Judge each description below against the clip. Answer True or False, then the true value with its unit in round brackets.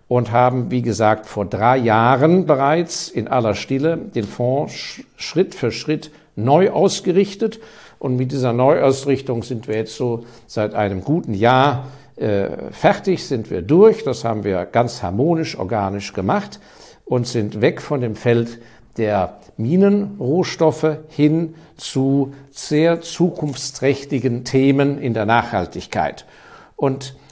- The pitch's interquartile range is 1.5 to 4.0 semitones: False (5.0 semitones)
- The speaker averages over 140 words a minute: False (130 wpm)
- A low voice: True (130 Hz)